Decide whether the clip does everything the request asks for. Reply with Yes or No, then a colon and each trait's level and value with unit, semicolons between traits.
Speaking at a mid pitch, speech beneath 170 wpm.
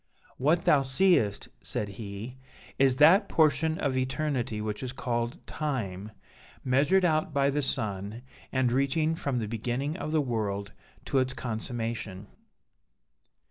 No: low, 130 Hz; slow, 135 wpm